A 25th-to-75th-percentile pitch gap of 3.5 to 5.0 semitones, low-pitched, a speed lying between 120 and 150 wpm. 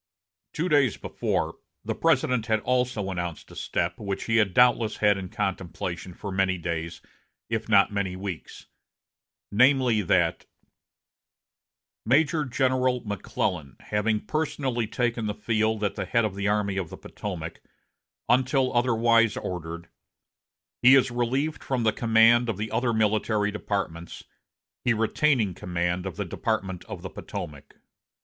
Yes: average, 4.1 semitones; low, 110 Hz; average, 140 wpm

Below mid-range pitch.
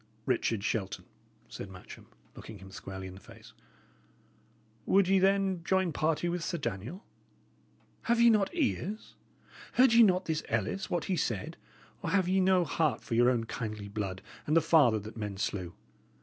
No: medium, 155 Hz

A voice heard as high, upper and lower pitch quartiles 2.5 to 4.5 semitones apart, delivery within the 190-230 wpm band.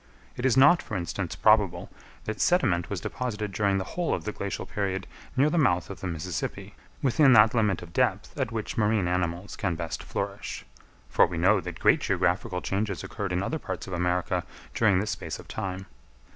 No: low, 100 Hz; average, 3.7 semitones; average, 195 wpm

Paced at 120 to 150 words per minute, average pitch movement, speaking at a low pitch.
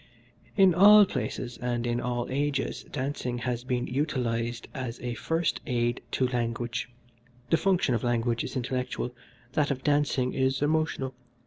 Yes: average, 145 wpm; average, 3.2 semitones; low, 125 Hz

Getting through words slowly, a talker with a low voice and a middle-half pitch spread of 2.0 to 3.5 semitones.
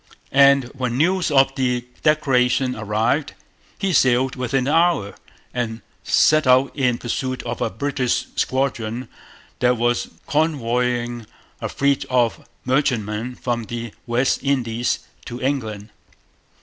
Yes: slow, 125 wpm; low, 125 Hz; narrow, 2.6 semitones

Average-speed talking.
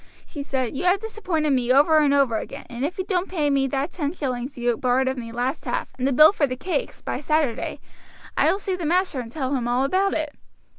No: fast, 245 wpm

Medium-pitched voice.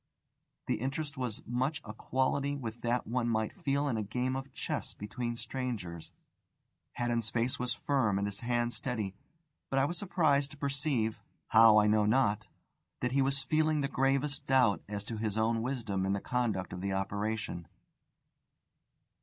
No: low, 120 Hz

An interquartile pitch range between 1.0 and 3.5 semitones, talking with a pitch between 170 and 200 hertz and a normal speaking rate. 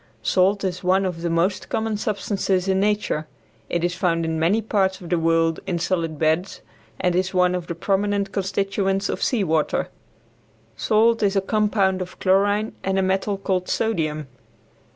Yes: average, 2.7 semitones; high, 190 Hz; average, 175 wpm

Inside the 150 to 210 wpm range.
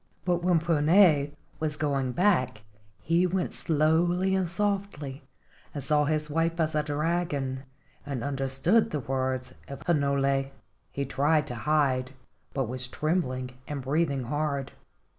No: slow, 135 wpm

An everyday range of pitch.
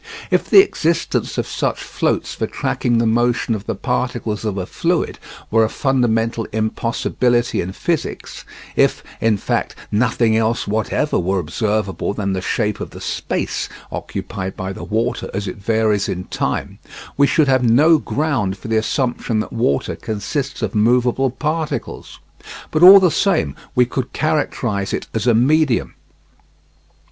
Yes: average, 3.7 semitones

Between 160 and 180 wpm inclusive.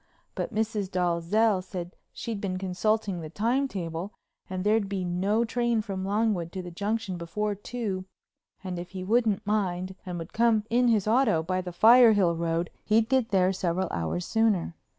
Yes: average, 170 wpm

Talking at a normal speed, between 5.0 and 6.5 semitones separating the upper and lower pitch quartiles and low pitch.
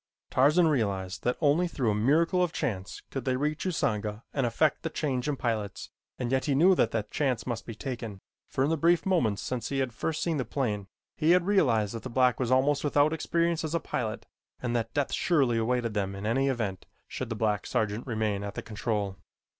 No: fast, 215 wpm; wide, 5.5 semitones; low, 125 Hz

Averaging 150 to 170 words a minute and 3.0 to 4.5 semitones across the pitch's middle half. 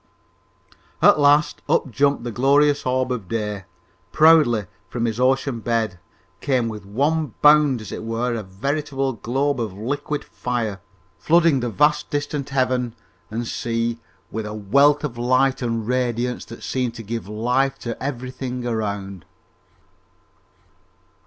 No: average, 140 wpm; average, 3.5 semitones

